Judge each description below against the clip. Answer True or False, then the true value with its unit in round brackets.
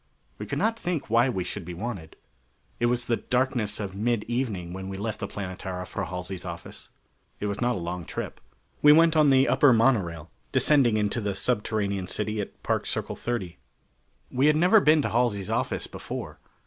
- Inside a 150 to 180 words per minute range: False (190 wpm)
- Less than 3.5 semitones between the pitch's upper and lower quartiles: False (4.9 semitones)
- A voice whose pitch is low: True (110 Hz)